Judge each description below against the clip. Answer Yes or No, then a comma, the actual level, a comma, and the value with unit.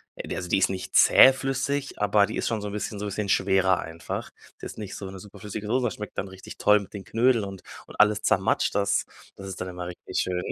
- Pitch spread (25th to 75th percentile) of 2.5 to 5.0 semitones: No, narrow, 2.1 semitones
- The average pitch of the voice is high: No, low, 100 Hz